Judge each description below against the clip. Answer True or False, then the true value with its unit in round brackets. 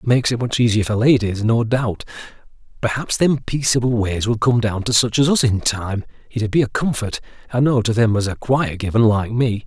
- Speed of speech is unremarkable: False (225 wpm)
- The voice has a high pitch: False (115 Hz)